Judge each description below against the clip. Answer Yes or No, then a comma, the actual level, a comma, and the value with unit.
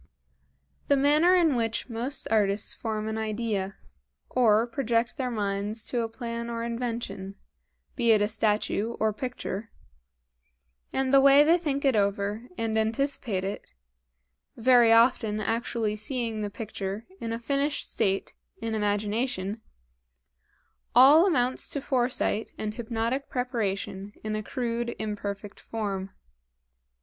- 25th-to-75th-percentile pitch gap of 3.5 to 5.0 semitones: No, average, 2.9 semitones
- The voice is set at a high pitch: Yes, high, 225 Hz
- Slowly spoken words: Yes, slow, 130 wpm